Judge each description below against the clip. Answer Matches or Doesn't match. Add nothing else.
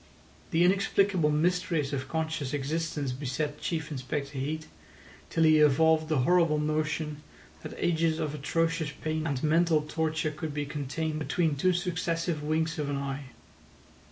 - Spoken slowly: Doesn't match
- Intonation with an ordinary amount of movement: Doesn't match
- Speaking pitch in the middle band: Matches